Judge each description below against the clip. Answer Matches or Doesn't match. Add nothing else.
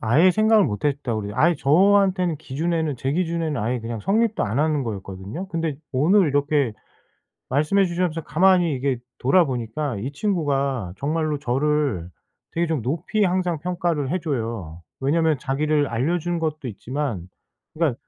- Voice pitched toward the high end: Doesn't match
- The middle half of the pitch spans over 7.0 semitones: Doesn't match